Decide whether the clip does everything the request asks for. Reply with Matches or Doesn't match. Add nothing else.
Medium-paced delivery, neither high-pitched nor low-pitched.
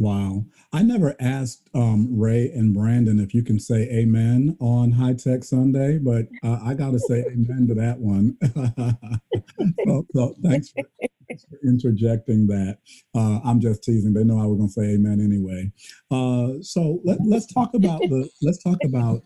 Doesn't match